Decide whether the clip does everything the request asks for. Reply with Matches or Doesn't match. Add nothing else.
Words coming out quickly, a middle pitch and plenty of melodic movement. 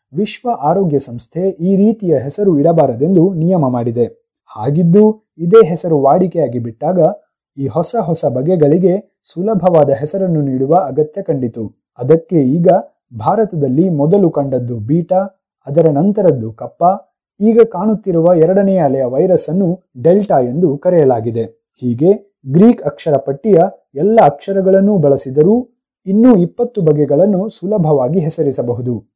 Matches